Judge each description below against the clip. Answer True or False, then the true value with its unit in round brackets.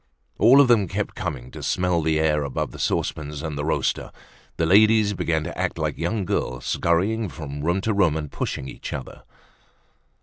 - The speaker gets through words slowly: False (190 wpm)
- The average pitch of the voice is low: True (85 Hz)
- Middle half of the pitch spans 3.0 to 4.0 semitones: False (4.8 semitones)